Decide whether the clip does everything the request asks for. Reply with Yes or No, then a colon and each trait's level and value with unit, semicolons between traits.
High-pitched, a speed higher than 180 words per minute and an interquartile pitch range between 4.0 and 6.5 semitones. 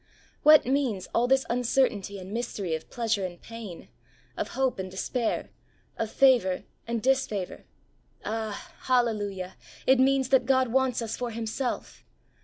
No: high, 235 Hz; average, 145 wpm; average, 4.3 semitones